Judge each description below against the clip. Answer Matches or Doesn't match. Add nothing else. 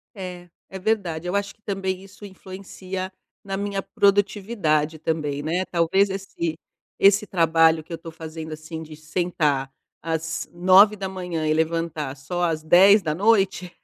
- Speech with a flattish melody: Doesn't match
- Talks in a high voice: Doesn't match